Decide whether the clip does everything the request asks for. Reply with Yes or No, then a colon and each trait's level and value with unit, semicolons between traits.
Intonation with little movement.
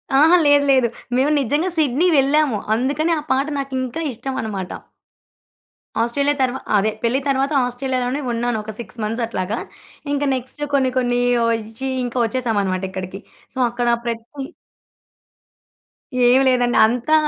No: average, 3.1 semitones